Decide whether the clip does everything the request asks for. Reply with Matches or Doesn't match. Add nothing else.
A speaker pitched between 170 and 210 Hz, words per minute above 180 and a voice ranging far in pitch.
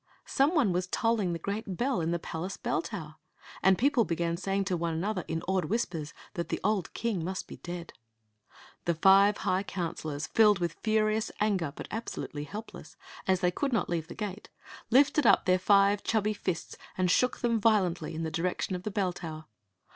Doesn't match